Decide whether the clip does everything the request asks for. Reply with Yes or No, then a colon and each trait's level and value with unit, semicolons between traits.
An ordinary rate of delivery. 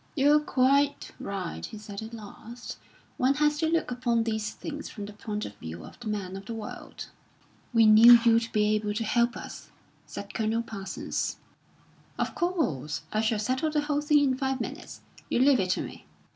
Yes: average, 190 wpm